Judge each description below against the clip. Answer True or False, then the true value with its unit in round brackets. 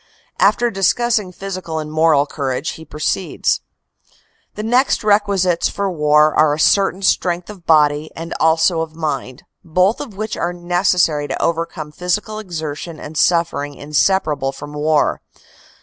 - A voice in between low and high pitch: True (165 Hz)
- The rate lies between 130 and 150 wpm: True (145 wpm)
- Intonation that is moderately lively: True (4.0 semitones)